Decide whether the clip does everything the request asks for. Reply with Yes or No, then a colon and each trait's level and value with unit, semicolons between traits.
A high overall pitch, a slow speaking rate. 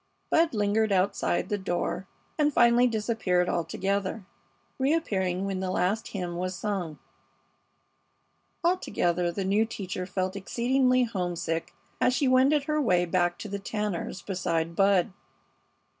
Yes: high, 195 Hz; slow, 130 wpm